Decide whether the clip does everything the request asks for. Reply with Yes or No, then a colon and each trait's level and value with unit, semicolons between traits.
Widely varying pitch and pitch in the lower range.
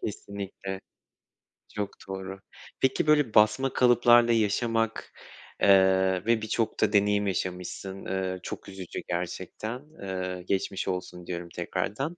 No: average, 3.3 semitones; low, 100 Hz